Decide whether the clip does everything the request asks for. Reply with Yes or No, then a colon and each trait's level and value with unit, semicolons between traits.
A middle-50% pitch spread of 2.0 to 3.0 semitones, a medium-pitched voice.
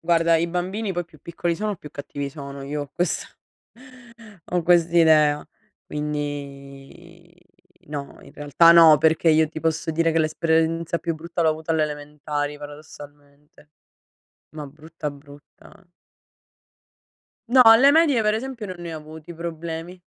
Yes: narrow, 2.5 semitones; medium, 160 Hz